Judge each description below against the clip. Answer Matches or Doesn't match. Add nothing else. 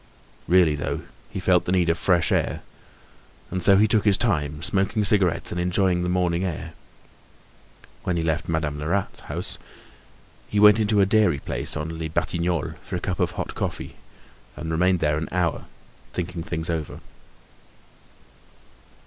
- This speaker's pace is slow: Doesn't match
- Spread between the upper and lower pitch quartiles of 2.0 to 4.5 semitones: Matches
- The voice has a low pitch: Matches